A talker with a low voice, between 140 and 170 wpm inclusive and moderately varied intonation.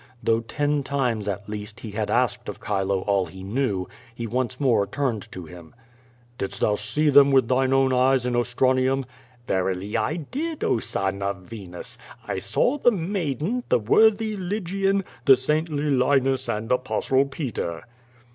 No: low, 125 Hz; average, 160 wpm; wide, 5.8 semitones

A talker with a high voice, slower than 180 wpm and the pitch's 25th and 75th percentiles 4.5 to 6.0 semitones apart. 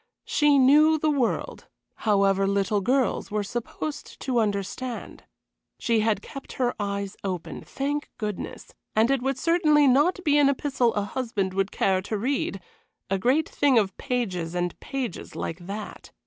Yes: high, 235 Hz; average, 155 wpm; wide, 5.6 semitones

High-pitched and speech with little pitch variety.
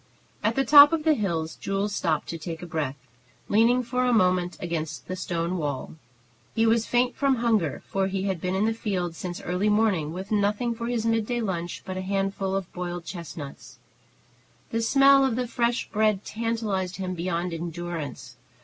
No: high, 195 Hz; average, 4.7 semitones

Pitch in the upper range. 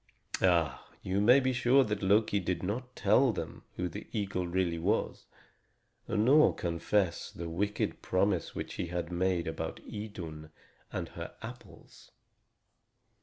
No: very low, 95 Hz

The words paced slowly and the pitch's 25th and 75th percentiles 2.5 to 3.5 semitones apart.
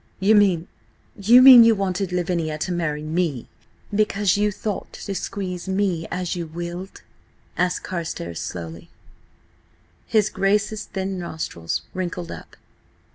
Yes: slow, 120 wpm; average, 3.2 semitones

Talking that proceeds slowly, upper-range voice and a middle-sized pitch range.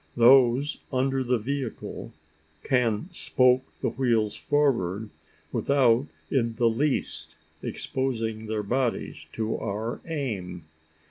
No: slow, 105 wpm; low, 120 Hz; average, 3.3 semitones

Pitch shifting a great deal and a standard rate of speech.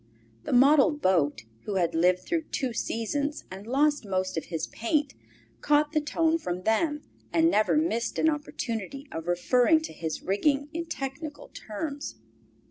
Yes: wide, 7.8 semitones; average, 155 wpm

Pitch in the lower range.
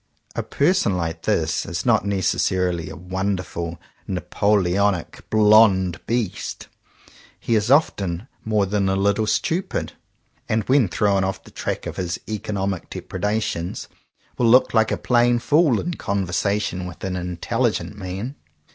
Yes: low, 100 Hz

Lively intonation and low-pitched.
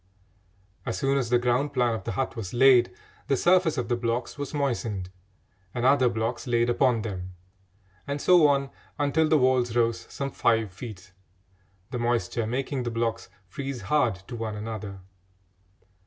No: average, 3.3 semitones; low, 120 Hz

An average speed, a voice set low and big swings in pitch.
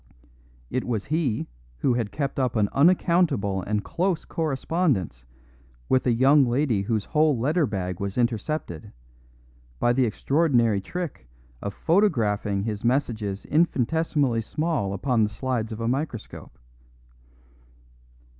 No: slow, 125 wpm; low, 120 Hz; wide, 6.3 semitones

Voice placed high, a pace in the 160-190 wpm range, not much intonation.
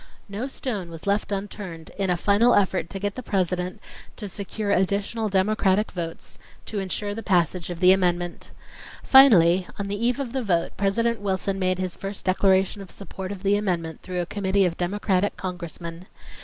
Yes: high, 195 Hz; average, 180 wpm; narrow, 2.1 semitones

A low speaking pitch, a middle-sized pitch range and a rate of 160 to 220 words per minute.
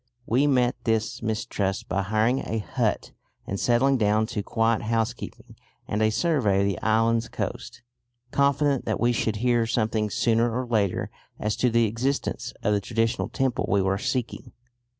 No: low, 115 Hz; narrow, 2.3 semitones; average, 165 wpm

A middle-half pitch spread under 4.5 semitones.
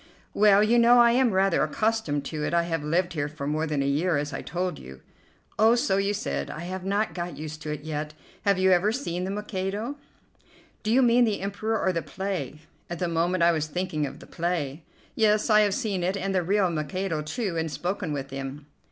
No: average, 5.0 semitones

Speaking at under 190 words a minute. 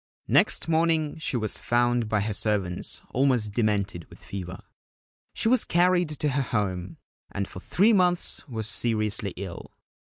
Yes: average, 150 wpm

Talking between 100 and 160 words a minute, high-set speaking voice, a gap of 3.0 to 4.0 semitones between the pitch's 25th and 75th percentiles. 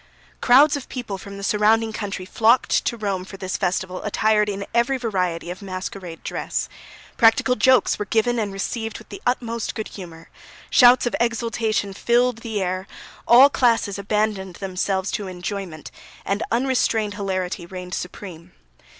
Yes: average, 150 wpm; high, 205 Hz; average, 3.6 semitones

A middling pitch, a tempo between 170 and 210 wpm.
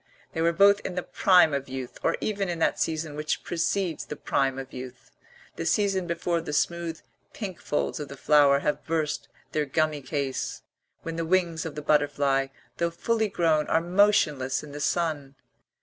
Yes: medium, 160 Hz; average, 180 wpm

